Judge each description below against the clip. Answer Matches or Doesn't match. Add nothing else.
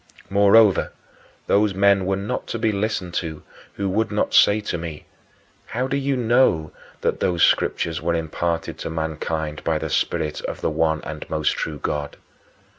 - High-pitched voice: Doesn't match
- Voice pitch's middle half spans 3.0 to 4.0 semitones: Doesn't match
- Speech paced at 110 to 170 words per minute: Matches